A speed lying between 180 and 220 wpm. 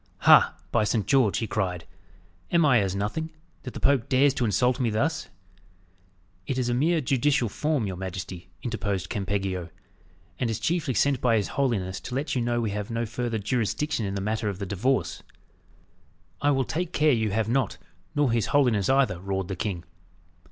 Yes: average, 185 wpm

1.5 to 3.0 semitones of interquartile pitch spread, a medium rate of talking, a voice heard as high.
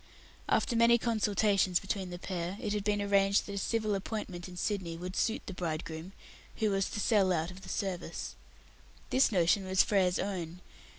Yes: narrow, 2.6 semitones; average, 185 wpm; high, 195 Hz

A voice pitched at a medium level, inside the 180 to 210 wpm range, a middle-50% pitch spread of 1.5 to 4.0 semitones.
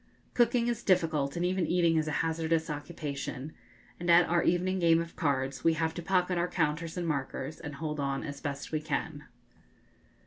Yes: medium, 160 Hz; average, 185 wpm; average, 2.9 semitones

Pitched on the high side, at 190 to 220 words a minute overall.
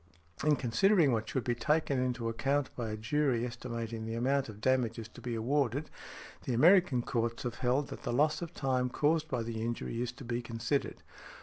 No: low, 125 Hz; average, 195 wpm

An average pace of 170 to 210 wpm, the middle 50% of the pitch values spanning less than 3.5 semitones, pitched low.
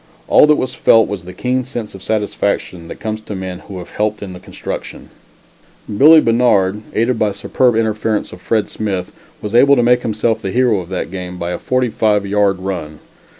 No: average, 200 wpm; average, 3.8 semitones; low, 105 Hz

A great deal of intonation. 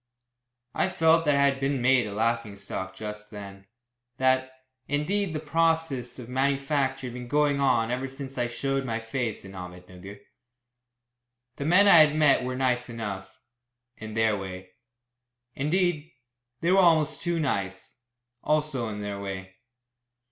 Yes: wide, 5.8 semitones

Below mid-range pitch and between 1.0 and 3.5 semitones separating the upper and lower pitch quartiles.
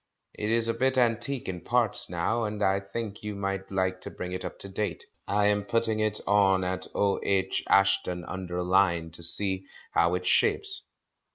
Yes: low, 100 Hz; narrow, 2.6 semitones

